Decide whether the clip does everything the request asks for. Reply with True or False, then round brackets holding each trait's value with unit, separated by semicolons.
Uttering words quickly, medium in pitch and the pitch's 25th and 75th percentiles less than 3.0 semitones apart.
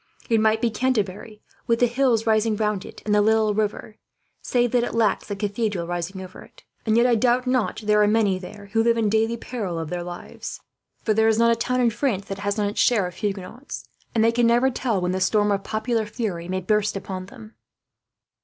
False (230 wpm; 215 Hz; 2.6 semitones)